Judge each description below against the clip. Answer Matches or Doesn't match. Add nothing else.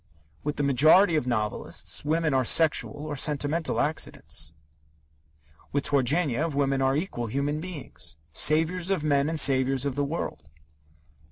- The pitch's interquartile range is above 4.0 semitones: Doesn't match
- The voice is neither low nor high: Matches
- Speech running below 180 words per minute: Matches